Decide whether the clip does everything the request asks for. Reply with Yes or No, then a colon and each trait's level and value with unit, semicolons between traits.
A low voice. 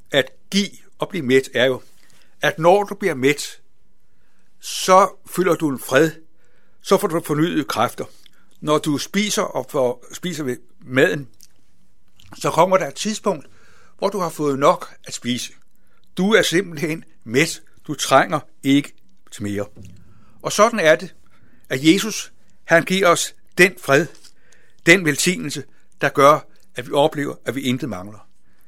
No: medium, 155 Hz